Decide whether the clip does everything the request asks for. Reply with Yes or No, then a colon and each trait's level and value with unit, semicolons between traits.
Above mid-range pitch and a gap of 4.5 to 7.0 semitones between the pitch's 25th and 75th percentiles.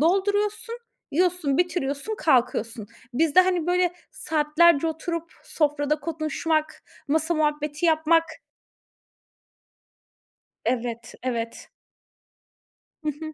No: very high, 310 Hz; average, 3.0 semitones